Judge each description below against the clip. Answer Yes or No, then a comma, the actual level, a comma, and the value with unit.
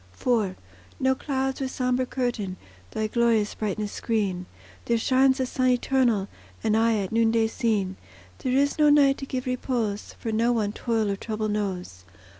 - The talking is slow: No, average, 165 wpm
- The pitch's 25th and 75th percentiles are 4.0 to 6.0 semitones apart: No, average, 3.5 semitones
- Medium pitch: No, high, 230 Hz